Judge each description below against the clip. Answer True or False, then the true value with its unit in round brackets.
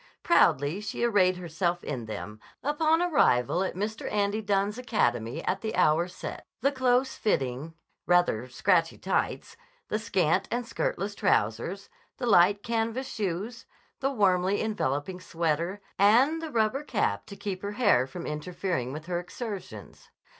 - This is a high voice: True (195 Hz)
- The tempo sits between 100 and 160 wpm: True (145 wpm)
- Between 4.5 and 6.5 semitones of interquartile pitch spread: True (5.2 semitones)